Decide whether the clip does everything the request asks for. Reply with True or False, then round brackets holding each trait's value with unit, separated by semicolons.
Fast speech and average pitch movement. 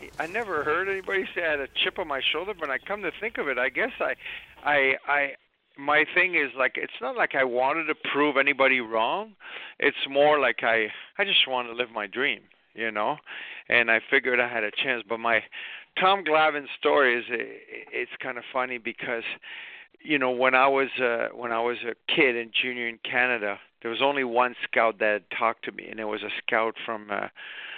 True (220 wpm; 4.3 semitones)